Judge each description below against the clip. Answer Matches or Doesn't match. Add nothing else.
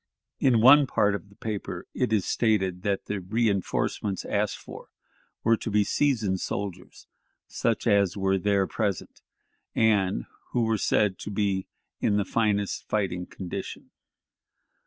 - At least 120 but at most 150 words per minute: Matches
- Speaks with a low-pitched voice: Matches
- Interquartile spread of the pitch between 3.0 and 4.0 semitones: Doesn't match